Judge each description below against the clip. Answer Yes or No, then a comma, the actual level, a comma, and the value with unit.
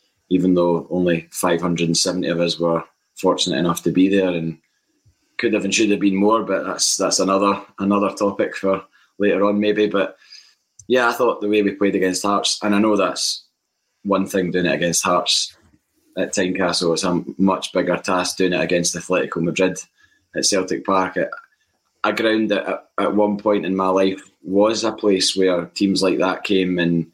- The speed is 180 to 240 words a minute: Yes, average, 185 wpm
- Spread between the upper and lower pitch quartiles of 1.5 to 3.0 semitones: Yes, narrow, 2.4 semitones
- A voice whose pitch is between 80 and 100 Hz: Yes, very low, 95 Hz